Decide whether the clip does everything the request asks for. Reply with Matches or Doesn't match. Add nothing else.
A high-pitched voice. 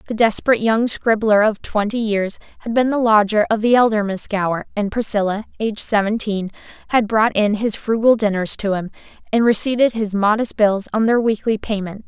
Matches